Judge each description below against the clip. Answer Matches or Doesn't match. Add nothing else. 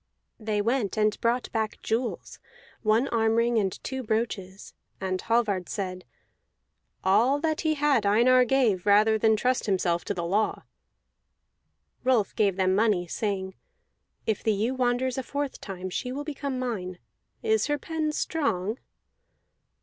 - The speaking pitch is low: Doesn't match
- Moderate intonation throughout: Matches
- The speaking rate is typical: Matches